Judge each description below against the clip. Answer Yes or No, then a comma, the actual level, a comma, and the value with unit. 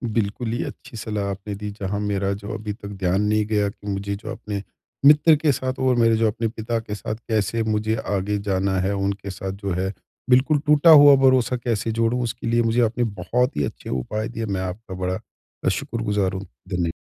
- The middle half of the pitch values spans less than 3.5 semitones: Yes, average, 2.9 semitones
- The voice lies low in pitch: Yes, low, 105 Hz